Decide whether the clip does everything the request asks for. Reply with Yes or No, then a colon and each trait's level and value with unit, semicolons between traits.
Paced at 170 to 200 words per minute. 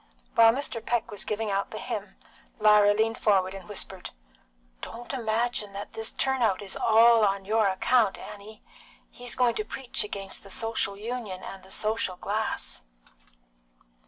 No: average, 155 wpm